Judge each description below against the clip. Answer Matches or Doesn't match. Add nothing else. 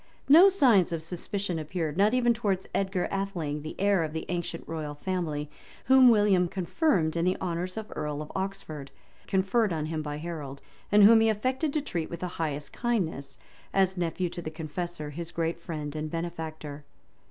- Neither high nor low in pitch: Matches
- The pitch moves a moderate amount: Matches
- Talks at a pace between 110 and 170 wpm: Doesn't match